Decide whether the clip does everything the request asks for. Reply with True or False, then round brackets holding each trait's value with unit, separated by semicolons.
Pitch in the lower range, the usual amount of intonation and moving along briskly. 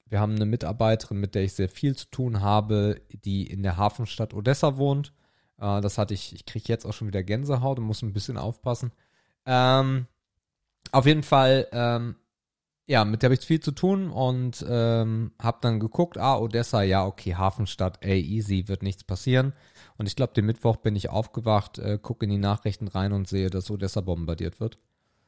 True (110 Hz; 3.9 semitones; 195 wpm)